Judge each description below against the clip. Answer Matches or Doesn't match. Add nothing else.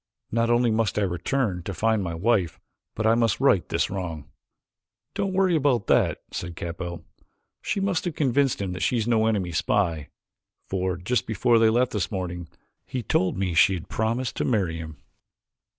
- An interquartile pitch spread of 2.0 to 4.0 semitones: Doesn't match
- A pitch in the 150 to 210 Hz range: Doesn't match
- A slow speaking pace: Doesn't match